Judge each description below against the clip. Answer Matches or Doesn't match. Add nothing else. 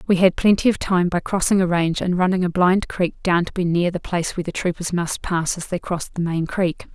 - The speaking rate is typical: Doesn't match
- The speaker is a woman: Matches